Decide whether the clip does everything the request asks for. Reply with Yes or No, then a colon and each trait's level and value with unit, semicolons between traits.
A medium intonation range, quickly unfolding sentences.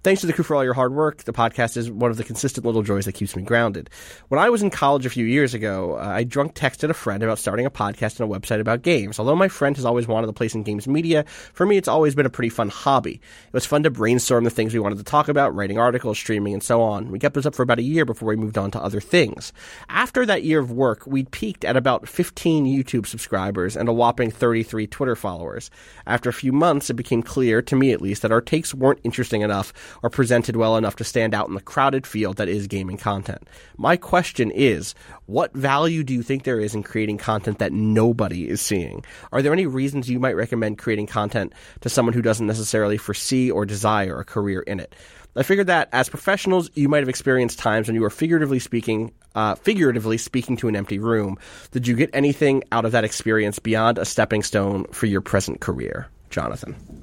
Yes: average, 4.0 semitones; fast, 240 wpm